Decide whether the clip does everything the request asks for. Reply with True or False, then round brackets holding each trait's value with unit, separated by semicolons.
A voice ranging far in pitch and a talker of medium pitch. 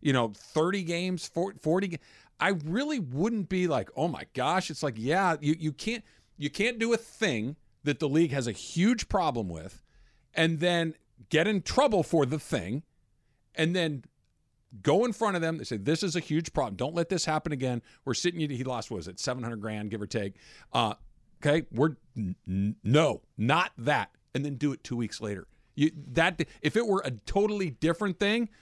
True (6.3 semitones; 155 Hz)